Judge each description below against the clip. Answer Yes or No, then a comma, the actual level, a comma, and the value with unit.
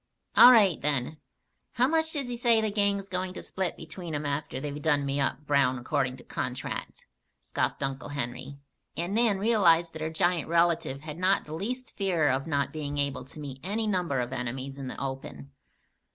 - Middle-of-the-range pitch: Yes, medium, 155 Hz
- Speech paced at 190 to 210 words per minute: Yes, average, 195 wpm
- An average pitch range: No, wide, 5.9 semitones